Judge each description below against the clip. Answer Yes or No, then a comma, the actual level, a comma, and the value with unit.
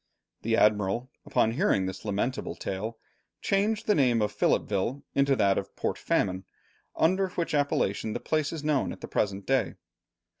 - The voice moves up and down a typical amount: No, wide, 7.0 semitones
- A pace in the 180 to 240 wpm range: No, average, 160 wpm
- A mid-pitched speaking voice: No, low, 120 Hz